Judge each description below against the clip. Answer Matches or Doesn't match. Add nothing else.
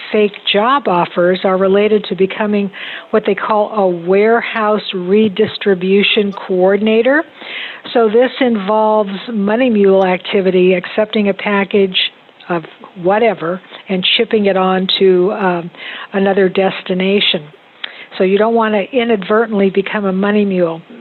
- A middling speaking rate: Doesn't match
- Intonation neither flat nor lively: Doesn't match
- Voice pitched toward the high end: Matches